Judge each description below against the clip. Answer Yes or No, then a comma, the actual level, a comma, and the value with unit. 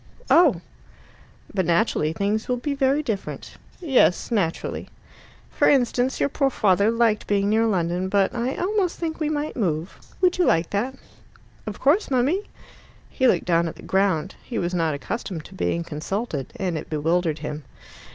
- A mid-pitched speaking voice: No, high, 205 Hz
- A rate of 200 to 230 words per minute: No, average, 165 wpm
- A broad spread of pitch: Yes, wide, 7.5 semitones